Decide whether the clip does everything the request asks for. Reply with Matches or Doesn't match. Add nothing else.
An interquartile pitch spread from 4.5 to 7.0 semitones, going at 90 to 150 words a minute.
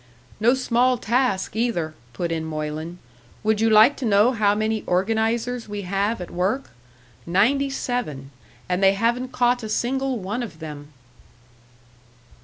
Matches